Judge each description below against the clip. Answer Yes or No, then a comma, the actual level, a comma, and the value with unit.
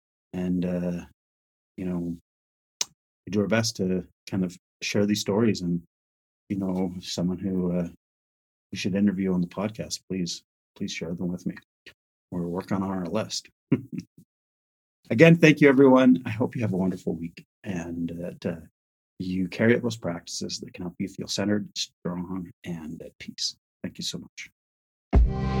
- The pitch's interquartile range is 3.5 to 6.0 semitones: No, narrow, 2.5 semitones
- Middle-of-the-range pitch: No, very low, 90 Hz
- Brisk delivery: No, average, 165 wpm